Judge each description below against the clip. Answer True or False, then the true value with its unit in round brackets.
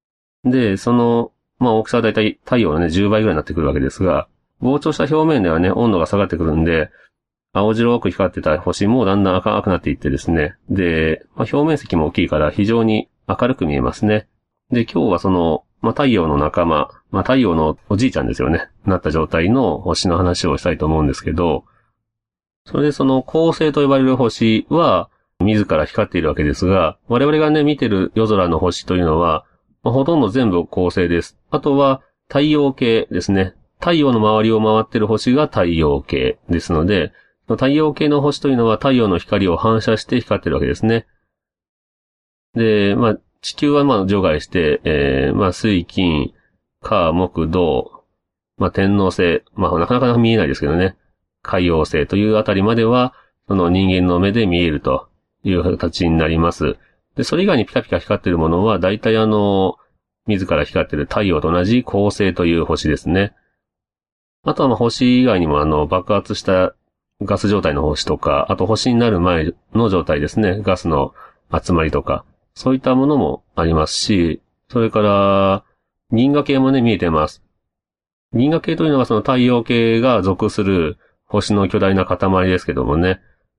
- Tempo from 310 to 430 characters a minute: True (340 characters per minute)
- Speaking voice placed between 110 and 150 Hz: False (100 Hz)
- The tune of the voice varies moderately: True (5.0 semitones)